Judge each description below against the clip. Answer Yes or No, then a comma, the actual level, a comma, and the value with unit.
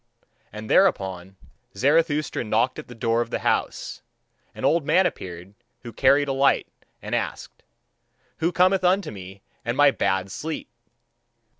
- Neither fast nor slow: Yes, average, 145 wpm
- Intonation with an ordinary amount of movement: No, wide, 8.3 semitones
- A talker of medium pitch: No, low, 130 Hz